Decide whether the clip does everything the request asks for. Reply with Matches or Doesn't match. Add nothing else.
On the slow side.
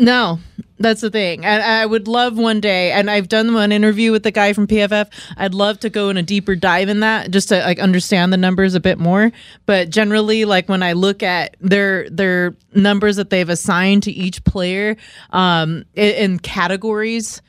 Doesn't match